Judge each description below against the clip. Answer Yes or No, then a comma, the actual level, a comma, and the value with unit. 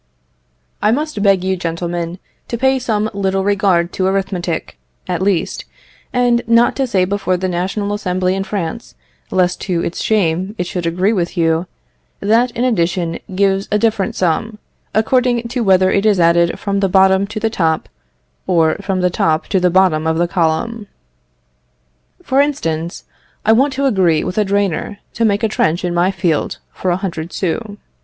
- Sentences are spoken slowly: No, average, 180 wpm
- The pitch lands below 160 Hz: No, high, 190 Hz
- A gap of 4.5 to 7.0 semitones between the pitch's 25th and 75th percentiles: No, average, 3.6 semitones